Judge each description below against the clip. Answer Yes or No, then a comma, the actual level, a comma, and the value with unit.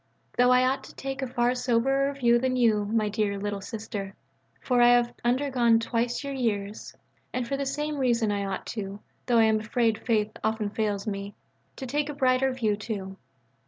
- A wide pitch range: No, average, 3.3 semitones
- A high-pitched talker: Yes, high, 235 Hz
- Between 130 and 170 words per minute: No, average, 195 wpm